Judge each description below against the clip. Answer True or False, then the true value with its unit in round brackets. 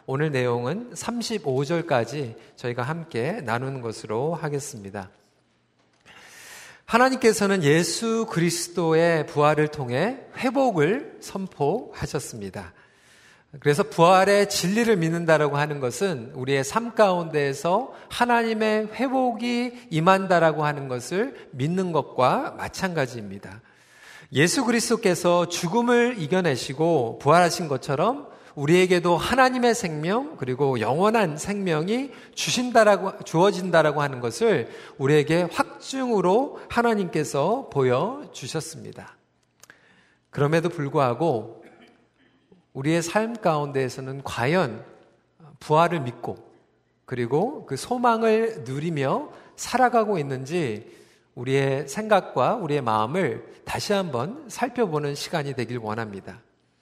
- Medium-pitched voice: True (165 Hz)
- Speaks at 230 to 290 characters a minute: True (270 characters per minute)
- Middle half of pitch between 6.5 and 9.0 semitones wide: True (7.7 semitones)